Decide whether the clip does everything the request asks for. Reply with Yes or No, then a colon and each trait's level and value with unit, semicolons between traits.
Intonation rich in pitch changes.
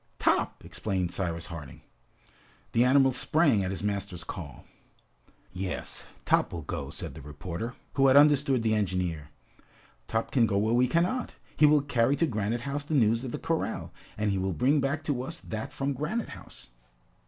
Yes: wide, 6.7 semitones